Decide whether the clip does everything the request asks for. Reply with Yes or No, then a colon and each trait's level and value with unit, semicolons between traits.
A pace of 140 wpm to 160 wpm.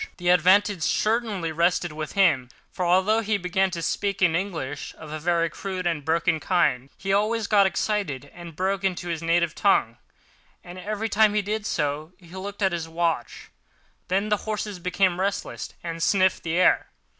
No: average, 175 wpm